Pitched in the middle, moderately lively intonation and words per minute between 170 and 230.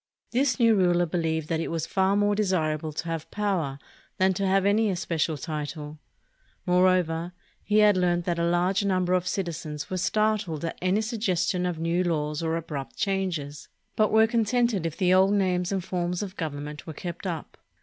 Yes: medium, 180 Hz; average, 3.2 semitones; average, 190 wpm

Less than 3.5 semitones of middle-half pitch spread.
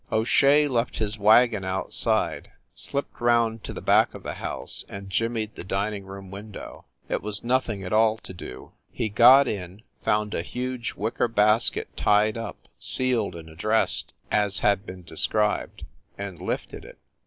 Yes: average, 2.9 semitones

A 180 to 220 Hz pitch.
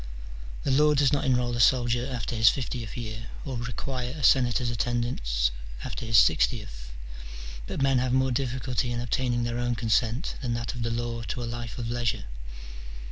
No: low, 120 Hz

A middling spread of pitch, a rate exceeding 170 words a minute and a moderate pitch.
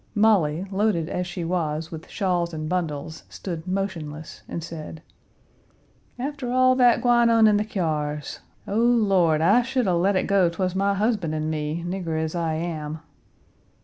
No: average, 4.6 semitones; average, 165 wpm; medium, 180 Hz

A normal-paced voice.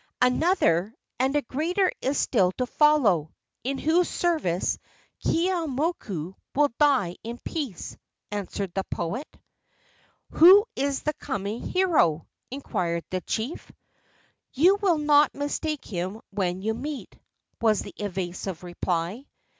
No: slow, 120 wpm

